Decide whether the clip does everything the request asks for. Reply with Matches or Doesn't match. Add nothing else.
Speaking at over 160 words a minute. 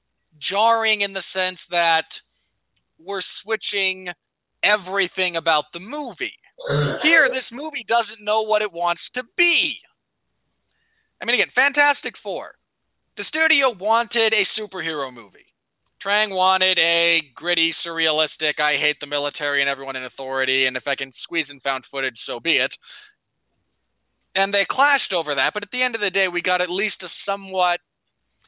Doesn't match